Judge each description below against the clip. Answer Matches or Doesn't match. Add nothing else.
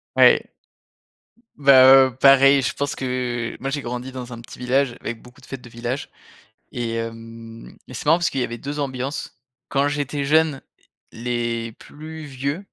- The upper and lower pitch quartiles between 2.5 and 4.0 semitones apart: Matches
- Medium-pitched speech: Doesn't match